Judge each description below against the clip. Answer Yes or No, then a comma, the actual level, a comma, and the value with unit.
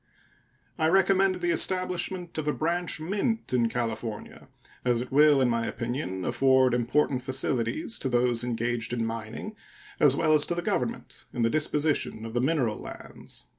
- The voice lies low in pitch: Yes, low, 130 Hz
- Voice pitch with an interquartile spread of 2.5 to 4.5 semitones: No, wide, 5.5 semitones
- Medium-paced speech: Yes, average, 165 wpm